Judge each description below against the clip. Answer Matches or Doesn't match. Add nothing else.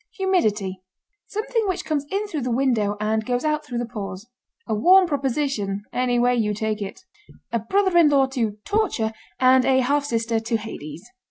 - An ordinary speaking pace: Matches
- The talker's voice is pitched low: Doesn't match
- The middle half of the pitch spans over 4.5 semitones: Matches